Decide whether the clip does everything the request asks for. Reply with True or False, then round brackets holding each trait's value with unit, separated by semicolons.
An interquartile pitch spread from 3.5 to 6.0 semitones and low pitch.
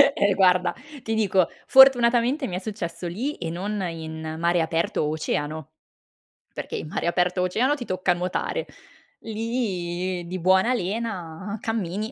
False (4.5 semitones; 185 Hz)